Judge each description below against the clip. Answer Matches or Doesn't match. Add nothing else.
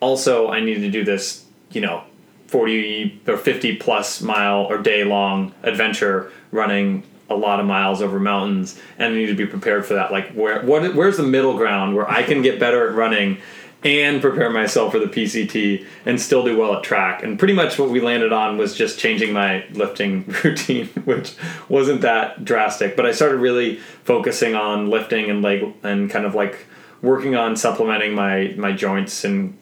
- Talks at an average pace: Matches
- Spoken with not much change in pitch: Matches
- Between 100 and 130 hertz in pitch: Matches